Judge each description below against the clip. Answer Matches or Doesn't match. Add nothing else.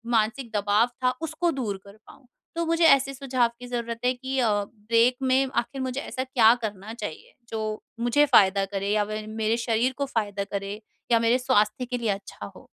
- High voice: Matches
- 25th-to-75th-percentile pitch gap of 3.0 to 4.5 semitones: Matches